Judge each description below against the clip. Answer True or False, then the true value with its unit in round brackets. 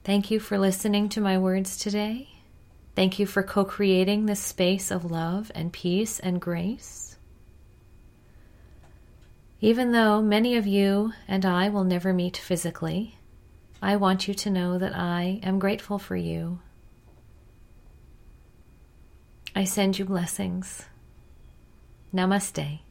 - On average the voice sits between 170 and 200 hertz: True (185 Hz)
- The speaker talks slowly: True (125 wpm)